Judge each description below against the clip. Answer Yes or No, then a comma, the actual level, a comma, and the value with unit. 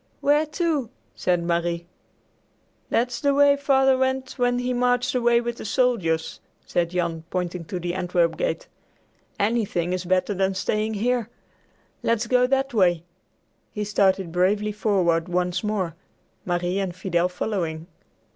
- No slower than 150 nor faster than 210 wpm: No, average, 140 wpm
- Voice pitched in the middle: No, high, 200 Hz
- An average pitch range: No, wide, 5.8 semitones